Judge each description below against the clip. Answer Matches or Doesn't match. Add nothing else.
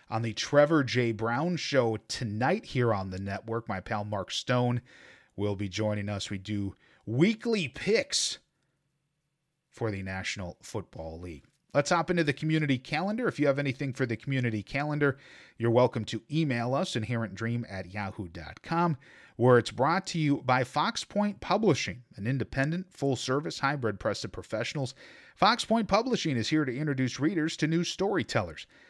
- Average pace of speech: Matches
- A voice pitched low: Matches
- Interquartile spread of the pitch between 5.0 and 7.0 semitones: Matches